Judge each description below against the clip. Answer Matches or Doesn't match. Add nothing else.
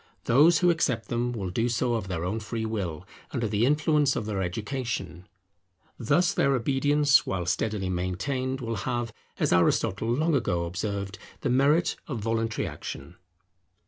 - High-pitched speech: Doesn't match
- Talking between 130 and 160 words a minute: Matches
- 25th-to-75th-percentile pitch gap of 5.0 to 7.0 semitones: Matches